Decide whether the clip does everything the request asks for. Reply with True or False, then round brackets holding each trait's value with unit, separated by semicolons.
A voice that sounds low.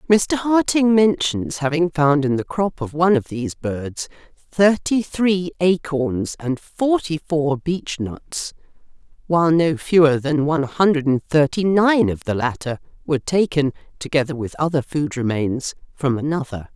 False (155 Hz)